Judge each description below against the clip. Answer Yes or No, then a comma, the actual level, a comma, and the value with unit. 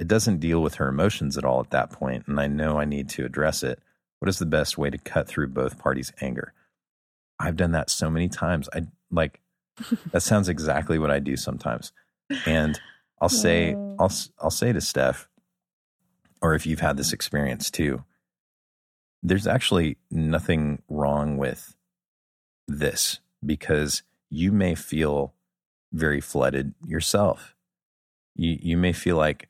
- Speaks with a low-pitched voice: Yes, very low, 75 Hz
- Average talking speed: Yes, average, 160 wpm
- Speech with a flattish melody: No, average, 3.8 semitones